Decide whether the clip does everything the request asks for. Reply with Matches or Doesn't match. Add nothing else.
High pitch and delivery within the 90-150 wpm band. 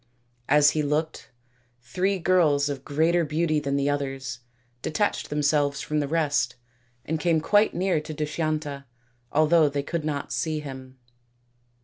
Doesn't match